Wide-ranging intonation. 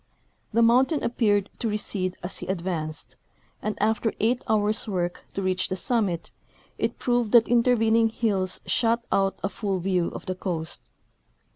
No: average, 3.7 semitones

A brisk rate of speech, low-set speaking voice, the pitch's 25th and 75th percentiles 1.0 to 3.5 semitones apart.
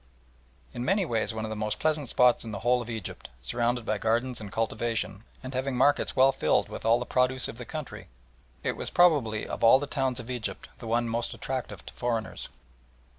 Yes: fast, 225 wpm; low, 120 Hz; average, 2.7 semitones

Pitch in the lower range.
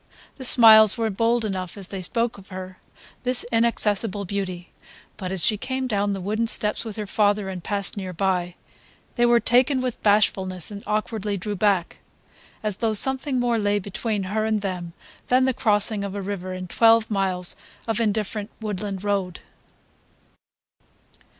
No: high, 205 Hz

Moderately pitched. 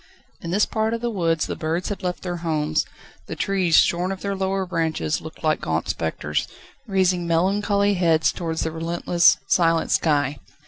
Yes: medium, 175 Hz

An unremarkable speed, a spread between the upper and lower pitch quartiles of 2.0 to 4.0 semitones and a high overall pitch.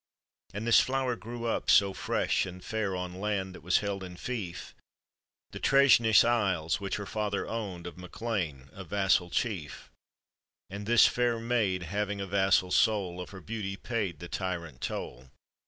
No: average, 170 wpm; average, 3.6 semitones; low, 100 Hz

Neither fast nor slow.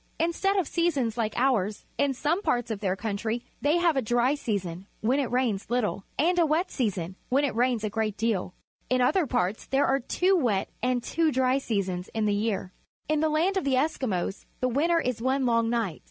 No: fast, 210 wpm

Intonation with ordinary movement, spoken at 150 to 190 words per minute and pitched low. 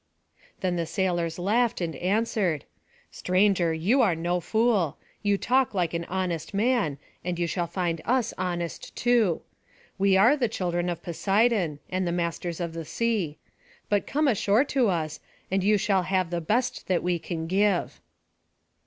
No: average, 3.8 semitones; average, 160 wpm; medium, 185 Hz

